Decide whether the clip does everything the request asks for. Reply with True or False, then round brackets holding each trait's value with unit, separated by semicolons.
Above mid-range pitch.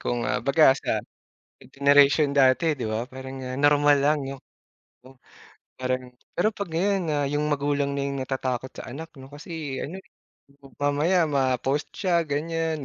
False (145 Hz)